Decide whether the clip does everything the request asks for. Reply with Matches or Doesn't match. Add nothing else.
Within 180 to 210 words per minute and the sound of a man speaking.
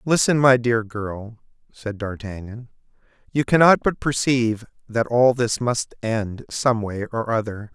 Doesn't match